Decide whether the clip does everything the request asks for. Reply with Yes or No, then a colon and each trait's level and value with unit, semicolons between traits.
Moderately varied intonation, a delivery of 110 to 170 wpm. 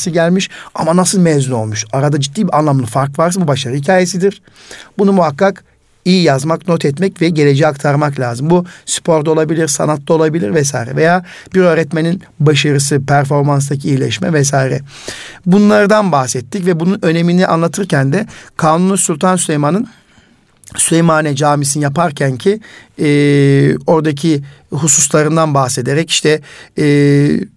Yes: average, 3.6 semitones; average, 125 wpm